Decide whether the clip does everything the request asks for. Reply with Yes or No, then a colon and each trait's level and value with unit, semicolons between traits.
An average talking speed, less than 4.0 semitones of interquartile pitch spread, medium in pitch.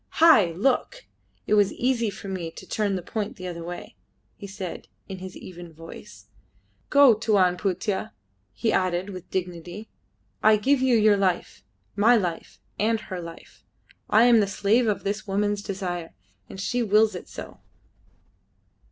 No: average, 160 wpm; average, 3.2 semitones; high, 200 Hz